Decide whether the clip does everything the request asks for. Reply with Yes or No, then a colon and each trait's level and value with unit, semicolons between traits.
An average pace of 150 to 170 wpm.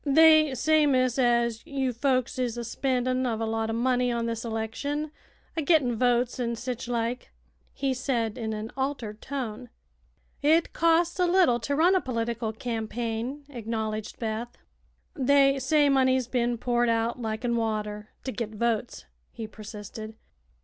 Yes: average, 155 wpm